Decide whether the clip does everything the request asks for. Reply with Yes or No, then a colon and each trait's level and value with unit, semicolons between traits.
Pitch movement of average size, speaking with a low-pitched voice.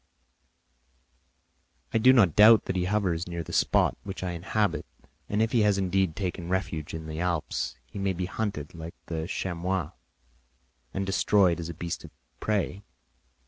Yes: average, 3.1 semitones; very low, 95 Hz